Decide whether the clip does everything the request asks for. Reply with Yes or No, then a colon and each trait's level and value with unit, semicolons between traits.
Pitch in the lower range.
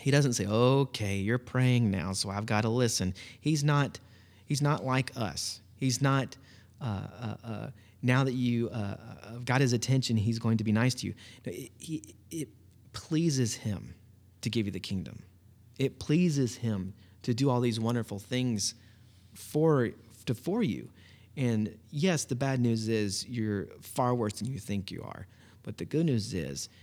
Yes: low, 115 Hz